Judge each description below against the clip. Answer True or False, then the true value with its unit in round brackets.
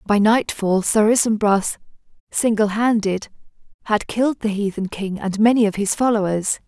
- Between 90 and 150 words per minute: True (145 wpm)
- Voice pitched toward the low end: False (210 Hz)